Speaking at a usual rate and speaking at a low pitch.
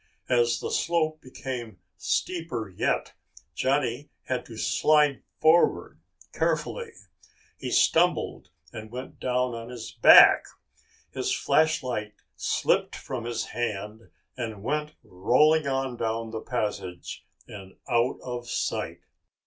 No: slow, 115 wpm; low, 125 Hz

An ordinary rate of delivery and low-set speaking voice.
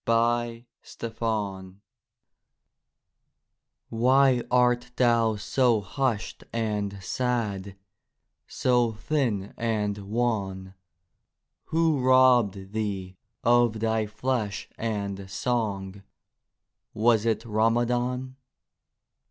No: slow, 80 wpm; low, 115 Hz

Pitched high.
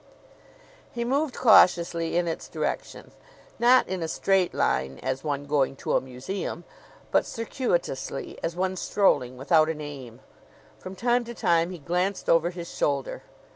No: medium, 170 Hz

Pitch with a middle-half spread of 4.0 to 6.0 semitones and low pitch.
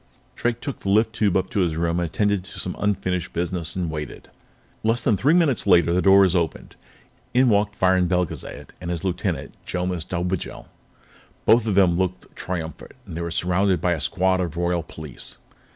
No: average, 2.9 semitones; very low, 90 Hz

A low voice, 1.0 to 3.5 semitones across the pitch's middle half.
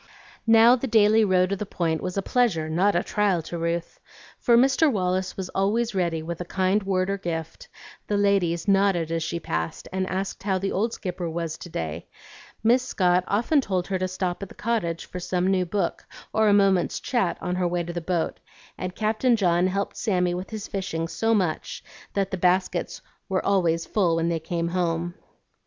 No: medium, 185 Hz; average, 2.9 semitones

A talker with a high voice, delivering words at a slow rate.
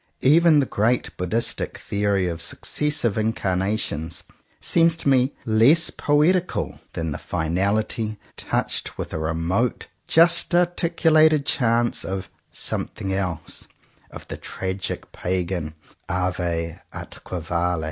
No: low, 105 Hz; slow, 110 wpm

